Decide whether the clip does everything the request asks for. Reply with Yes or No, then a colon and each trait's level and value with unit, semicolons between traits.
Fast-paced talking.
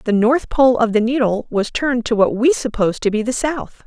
Yes: fast, 250 wpm